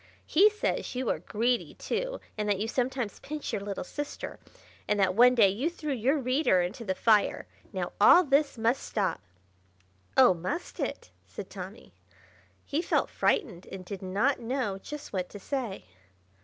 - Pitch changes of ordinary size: No, wide, 5.8 semitones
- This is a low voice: No, high, 230 Hz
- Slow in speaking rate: No, average, 170 wpm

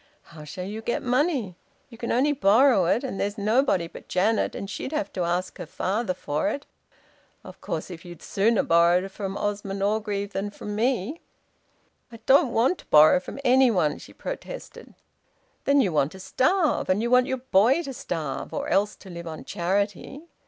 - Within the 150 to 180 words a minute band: No, average, 190 wpm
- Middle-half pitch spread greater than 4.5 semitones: Yes, wide, 5.6 semitones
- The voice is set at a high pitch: Yes, high, 205 Hz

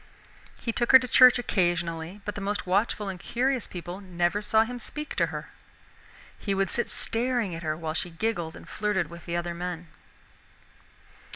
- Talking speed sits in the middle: Yes, average, 180 wpm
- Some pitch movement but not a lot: Yes, average, 4.7 semitones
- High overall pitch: Yes, high, 195 Hz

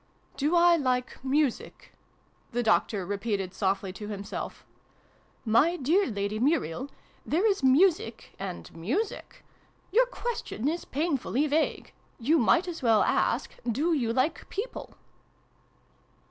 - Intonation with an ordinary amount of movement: No, wide, 7.5 semitones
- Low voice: No, very high, 260 Hz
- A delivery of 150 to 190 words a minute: No, slow, 135 wpm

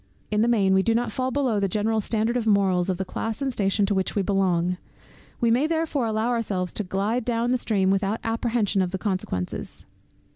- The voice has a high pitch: Yes, high, 215 Hz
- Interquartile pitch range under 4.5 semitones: Yes, average, 3.5 semitones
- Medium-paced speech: No, fast, 215 wpm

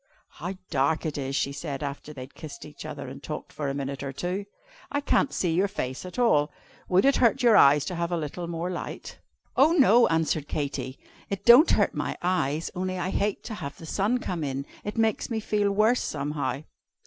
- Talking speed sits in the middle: No, fast, 215 wpm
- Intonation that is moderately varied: No, wide, 6.2 semitones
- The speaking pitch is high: No, medium, 170 Hz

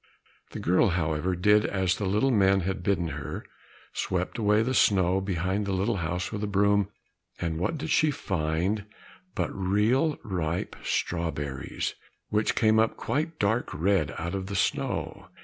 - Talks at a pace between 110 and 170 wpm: Yes, average, 160 wpm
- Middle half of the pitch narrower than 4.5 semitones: Yes, average, 3.2 semitones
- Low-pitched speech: Yes, very low, 95 Hz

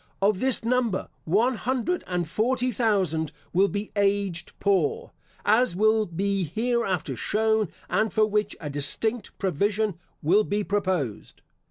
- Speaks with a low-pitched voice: No, high, 205 Hz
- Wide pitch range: No, average, 3.3 semitones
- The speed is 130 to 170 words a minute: Yes, slow, 135 wpm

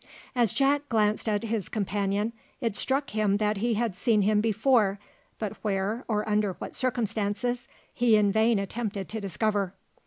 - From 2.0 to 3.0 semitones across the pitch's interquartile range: Yes, narrow, 2.4 semitones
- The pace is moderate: Yes, average, 160 wpm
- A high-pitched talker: Yes, high, 215 Hz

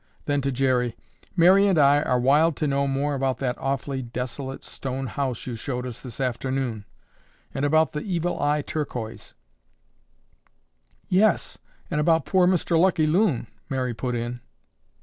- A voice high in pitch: No, low, 135 Hz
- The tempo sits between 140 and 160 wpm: Yes, average, 150 wpm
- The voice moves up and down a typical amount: Yes, average, 3.7 semitones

